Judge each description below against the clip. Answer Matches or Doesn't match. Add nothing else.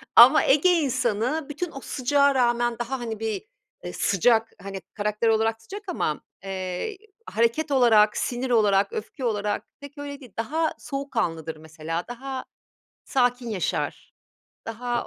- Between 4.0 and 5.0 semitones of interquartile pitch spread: Matches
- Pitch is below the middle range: Doesn't match